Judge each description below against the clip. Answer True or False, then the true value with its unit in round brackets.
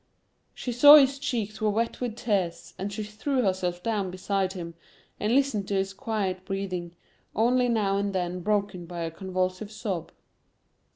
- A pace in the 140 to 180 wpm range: True (165 wpm)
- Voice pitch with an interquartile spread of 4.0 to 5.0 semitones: False (3.4 semitones)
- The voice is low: False (200 Hz)